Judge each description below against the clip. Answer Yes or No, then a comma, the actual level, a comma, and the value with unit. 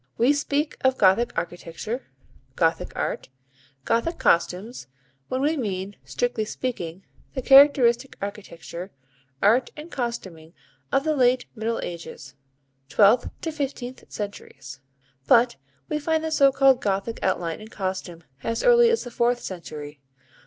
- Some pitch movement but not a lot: No, wide, 6.2 semitones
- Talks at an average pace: No, slow, 130 wpm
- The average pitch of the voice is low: No, high, 235 Hz